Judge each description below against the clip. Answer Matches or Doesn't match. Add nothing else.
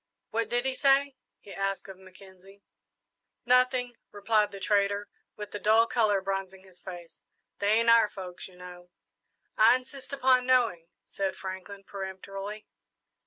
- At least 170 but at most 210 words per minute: Doesn't match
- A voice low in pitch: Doesn't match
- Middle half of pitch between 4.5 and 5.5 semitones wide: Doesn't match